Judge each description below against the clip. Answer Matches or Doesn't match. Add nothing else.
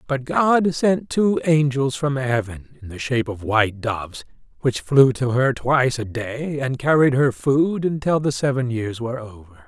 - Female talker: Doesn't match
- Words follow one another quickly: Doesn't match